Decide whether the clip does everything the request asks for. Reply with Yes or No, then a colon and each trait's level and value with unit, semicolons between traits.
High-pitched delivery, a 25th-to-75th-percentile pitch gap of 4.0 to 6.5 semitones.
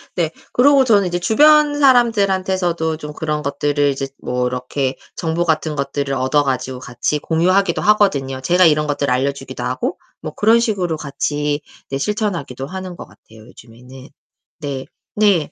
No: medium, 155 Hz; wide, 5.6 semitones